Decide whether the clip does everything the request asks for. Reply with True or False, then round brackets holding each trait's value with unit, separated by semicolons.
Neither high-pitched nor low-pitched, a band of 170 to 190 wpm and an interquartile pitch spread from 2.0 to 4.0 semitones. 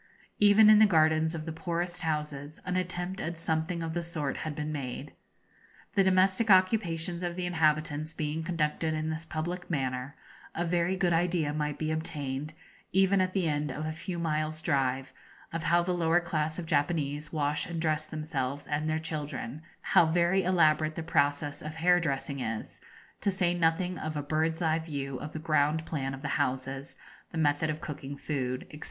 True (160 Hz; 185 wpm; 2.6 semitones)